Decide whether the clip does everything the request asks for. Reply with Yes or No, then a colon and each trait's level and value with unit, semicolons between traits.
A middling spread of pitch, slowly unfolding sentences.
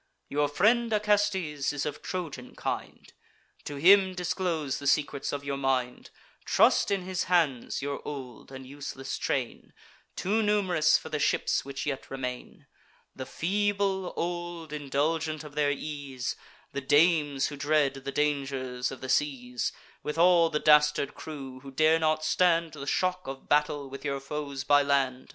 No: average, 3.7 semitones; average, 155 wpm